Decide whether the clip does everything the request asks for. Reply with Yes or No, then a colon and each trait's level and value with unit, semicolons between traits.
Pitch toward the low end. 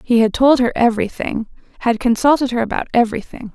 No: high, 235 Hz